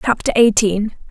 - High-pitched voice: Yes, high, 215 Hz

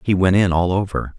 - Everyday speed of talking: No, fast, 255 wpm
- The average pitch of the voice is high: No, very low, 95 Hz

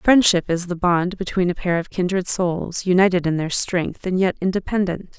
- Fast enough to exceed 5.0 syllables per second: No, 4.9 syllables/s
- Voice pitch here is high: No, medium, 180 Hz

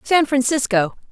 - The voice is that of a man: No, female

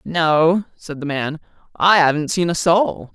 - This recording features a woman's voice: No, male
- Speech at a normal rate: Yes, average, 170 wpm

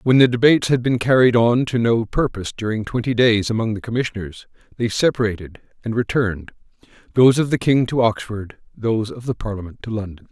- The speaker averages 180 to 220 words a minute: Yes, average, 185 wpm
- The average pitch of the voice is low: Yes, low, 115 Hz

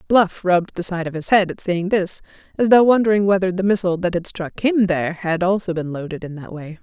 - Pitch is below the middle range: No, medium, 185 Hz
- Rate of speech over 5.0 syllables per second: Yes, 5.9 syllables/s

